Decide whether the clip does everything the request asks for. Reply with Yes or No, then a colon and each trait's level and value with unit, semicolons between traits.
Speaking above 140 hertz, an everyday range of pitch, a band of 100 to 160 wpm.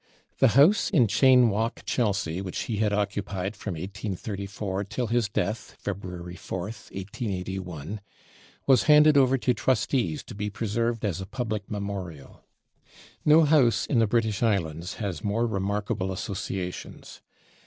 No: low, 105 Hz; average, 3.6 semitones; slow, 135 wpm